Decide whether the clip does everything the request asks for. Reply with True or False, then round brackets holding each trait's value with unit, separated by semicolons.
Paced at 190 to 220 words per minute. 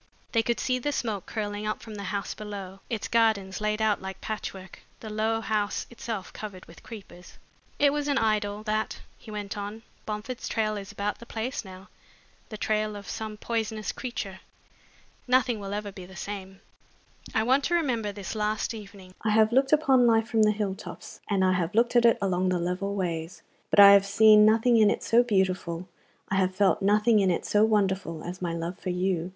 True (200 wpm)